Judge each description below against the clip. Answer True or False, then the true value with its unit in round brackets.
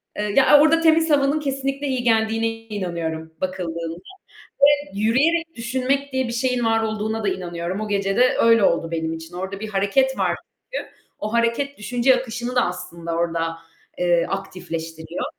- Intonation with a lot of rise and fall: True (6.8 semitones)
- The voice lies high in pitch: True (220 Hz)